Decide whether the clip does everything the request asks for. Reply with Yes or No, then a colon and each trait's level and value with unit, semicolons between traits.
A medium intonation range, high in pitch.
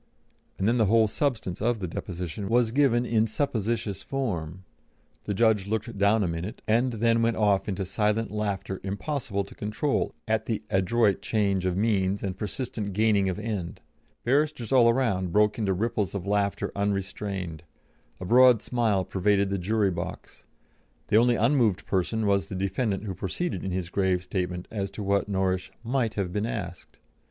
No: average, 3.1 semitones; low, 105 Hz